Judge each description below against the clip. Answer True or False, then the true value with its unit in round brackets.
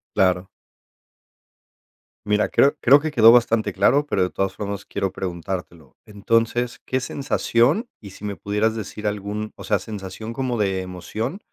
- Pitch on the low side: True (105 Hz)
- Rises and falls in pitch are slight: False (3.5 semitones)